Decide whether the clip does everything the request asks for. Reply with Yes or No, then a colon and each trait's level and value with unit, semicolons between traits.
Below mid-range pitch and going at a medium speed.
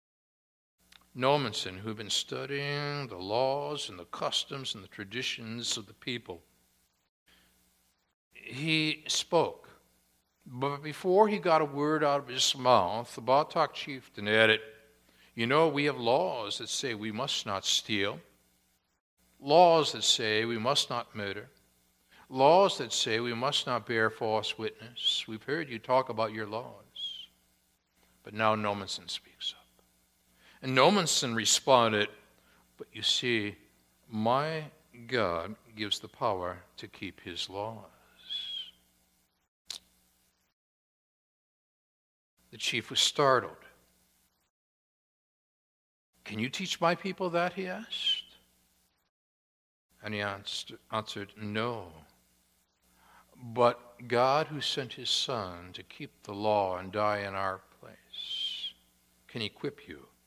No: low, 110 Hz; slow, 120 wpm